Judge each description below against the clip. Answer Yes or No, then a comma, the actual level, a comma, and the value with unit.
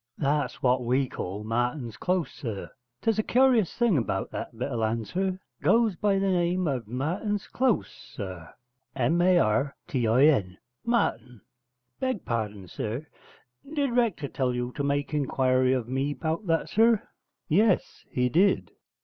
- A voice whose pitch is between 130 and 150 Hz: Yes, medium, 140 Hz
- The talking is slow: No, average, 160 wpm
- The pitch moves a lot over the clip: Yes, wide, 7.6 semitones